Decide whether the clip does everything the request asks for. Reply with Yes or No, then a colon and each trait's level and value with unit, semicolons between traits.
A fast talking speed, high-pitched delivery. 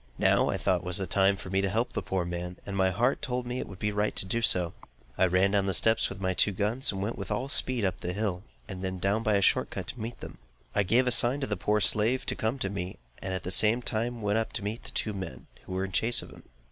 No: fast, 295 wpm; low, 100 Hz